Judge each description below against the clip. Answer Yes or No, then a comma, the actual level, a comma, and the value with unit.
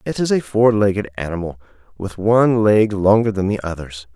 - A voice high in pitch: No, low, 100 Hz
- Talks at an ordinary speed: Yes, average, 190 wpm